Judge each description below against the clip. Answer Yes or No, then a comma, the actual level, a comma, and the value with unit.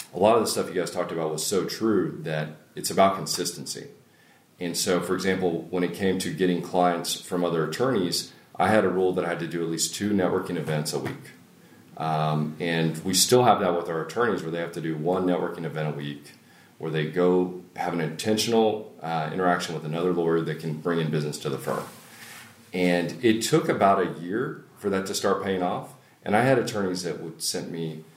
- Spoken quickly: Yes, fast, 220 wpm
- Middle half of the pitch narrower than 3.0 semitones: Yes, narrow, 2.5 semitones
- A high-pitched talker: No, very low, 85 Hz